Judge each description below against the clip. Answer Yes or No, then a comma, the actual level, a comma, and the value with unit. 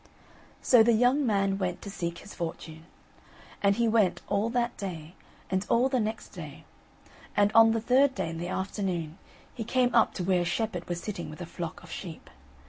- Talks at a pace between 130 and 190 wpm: No, average, 200 wpm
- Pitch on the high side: Yes, high, 200 Hz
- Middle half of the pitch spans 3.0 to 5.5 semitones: Yes, average, 4.7 semitones